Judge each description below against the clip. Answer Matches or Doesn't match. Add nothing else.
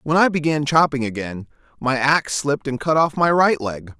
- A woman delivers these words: Doesn't match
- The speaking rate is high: Matches